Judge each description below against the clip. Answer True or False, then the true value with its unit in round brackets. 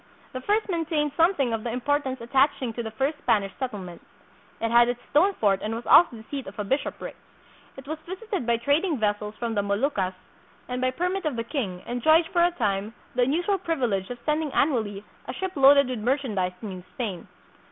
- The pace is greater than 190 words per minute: True (200 wpm)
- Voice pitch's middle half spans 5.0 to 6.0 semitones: True (5.6 semitones)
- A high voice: True (250 Hz)